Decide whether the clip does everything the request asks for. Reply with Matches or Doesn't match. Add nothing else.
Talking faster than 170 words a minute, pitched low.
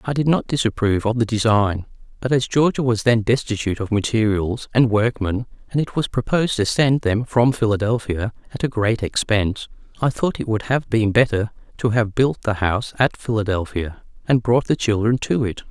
Matches